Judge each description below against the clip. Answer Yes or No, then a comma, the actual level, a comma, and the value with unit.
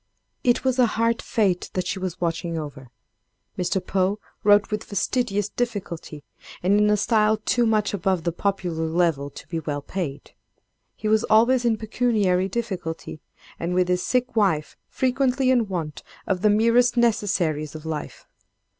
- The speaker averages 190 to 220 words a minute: No, average, 160 wpm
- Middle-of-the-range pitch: No, high, 195 Hz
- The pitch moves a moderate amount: Yes, average, 4.8 semitones